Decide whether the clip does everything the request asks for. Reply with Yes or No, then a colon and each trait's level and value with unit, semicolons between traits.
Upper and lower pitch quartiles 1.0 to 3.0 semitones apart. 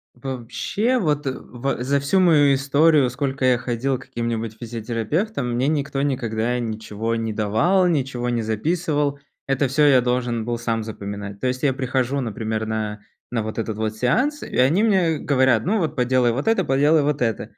No: average, 4.0 semitones